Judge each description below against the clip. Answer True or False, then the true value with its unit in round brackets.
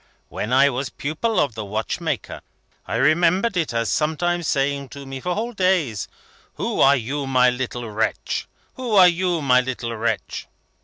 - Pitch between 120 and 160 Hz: True (140 Hz)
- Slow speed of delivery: False (165 wpm)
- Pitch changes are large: True (6.0 semitones)